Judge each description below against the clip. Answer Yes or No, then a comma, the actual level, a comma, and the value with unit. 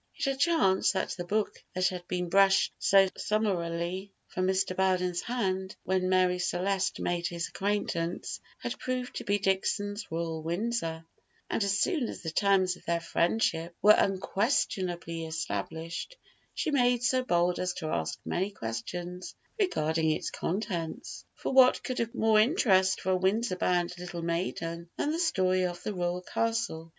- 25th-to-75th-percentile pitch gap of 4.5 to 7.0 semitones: No, average, 3.3 semitones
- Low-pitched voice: No, medium, 185 Hz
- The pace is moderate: Yes, average, 160 wpm